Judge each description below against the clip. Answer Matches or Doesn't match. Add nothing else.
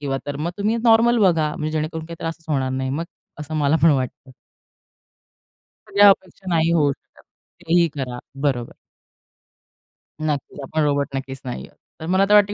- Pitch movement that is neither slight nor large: Matches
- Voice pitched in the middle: Matches